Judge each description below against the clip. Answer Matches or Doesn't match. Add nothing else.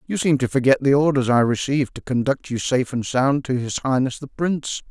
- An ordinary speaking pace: Doesn't match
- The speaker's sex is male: Matches